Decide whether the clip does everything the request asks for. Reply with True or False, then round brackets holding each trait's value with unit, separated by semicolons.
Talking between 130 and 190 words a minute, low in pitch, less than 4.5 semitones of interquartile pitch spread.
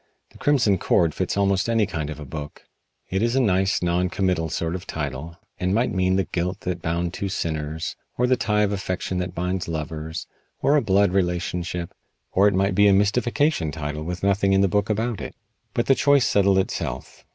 False (205 wpm; 95 Hz; 3.2 semitones)